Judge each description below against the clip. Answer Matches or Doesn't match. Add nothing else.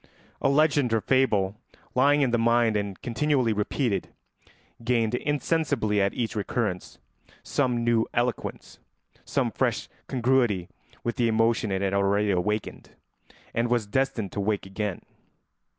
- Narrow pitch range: Doesn't match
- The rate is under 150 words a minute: Matches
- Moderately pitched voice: Doesn't match